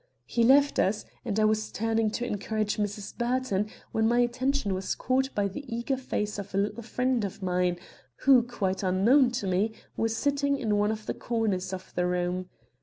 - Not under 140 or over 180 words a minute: No, average, 190 wpm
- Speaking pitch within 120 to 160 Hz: No, high, 215 Hz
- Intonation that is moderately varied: Yes, average, 3.7 semitones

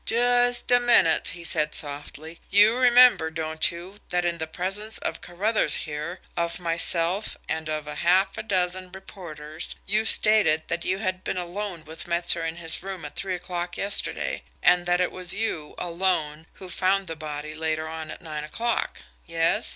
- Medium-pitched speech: Yes, medium, 175 Hz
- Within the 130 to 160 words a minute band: No, average, 175 wpm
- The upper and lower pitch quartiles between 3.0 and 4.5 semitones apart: Yes, average, 3.3 semitones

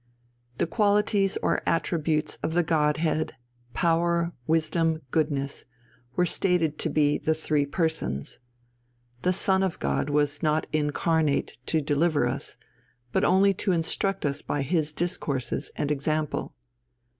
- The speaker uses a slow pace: Yes, slow, 130 wpm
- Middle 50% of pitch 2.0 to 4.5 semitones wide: Yes, average, 2.7 semitones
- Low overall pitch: No, medium, 160 Hz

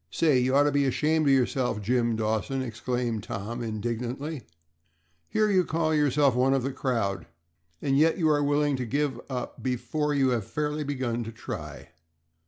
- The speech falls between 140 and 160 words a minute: No, average, 175 wpm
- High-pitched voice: No, low, 130 Hz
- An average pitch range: Yes, average, 3.7 semitones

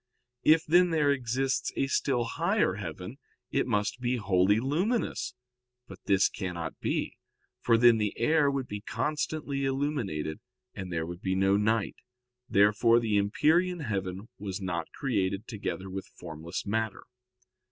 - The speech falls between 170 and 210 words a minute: No, average, 140 wpm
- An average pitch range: No, wide, 6.2 semitones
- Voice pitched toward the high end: No, low, 110 Hz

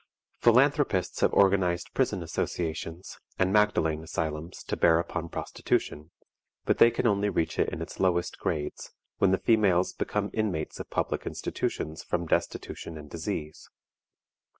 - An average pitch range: Yes, average, 4.0 semitones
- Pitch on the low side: Yes, very low, 90 Hz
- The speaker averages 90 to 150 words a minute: Yes, average, 140 wpm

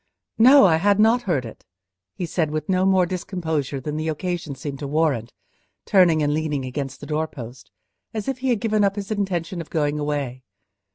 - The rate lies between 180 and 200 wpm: Yes, average, 190 wpm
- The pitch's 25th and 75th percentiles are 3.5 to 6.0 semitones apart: Yes, average, 4.8 semitones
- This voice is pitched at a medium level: Yes, medium, 160 Hz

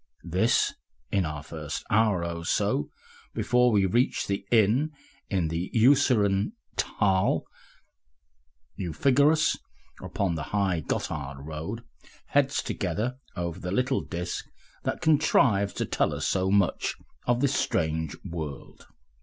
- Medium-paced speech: No, slow, 130 wpm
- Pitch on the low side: Yes, low, 100 Hz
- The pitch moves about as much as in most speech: No, wide, 6.4 semitones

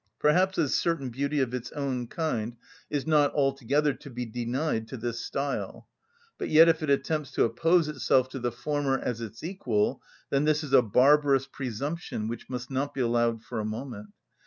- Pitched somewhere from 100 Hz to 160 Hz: Yes, low, 135 Hz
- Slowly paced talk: No, average, 185 wpm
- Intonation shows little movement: No, average, 3.8 semitones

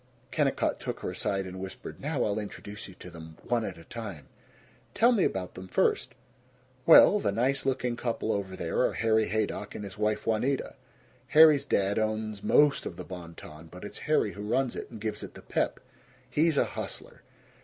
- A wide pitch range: No, average, 4.7 semitones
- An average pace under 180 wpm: No, average, 195 wpm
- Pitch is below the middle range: Yes, low, 110 Hz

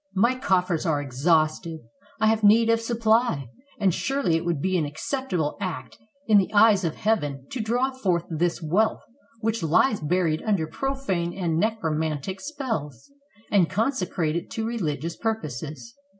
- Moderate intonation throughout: No, wide, 5.9 semitones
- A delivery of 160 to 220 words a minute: No, average, 150 wpm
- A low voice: No, medium, 185 Hz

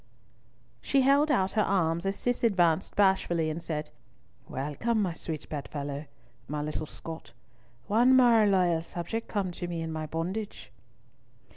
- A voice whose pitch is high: No, medium, 175 Hz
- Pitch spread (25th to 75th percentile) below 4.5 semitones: No, average, 5.0 semitones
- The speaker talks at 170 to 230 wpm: No, average, 145 wpm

